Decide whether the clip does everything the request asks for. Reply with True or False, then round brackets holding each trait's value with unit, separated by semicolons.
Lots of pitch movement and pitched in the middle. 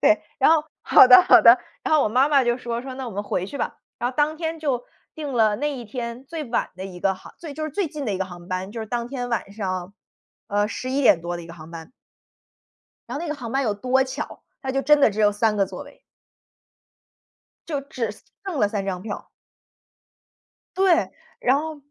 False (5.7 semitones; 240 Hz)